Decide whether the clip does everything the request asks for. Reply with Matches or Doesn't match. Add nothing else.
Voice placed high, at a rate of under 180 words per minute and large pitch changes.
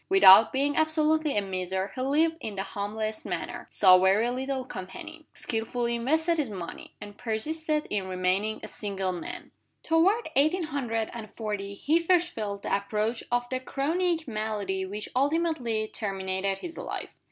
Matches